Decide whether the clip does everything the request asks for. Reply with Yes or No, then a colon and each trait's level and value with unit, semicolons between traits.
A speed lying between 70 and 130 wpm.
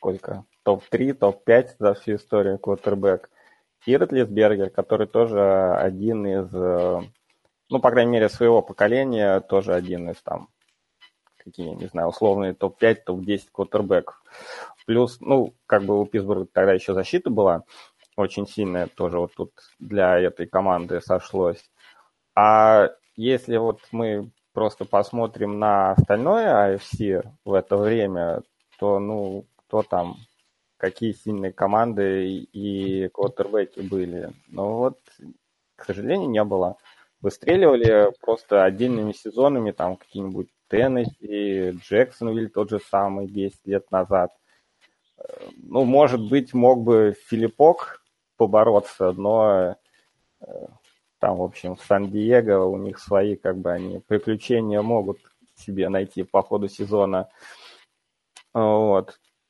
Yes: average, 120 wpm